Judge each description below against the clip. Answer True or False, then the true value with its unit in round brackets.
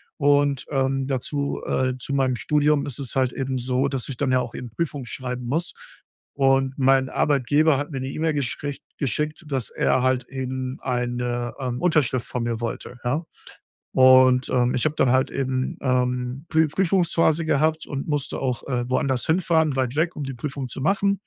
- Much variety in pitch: False (2.5 semitones)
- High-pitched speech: False (135 Hz)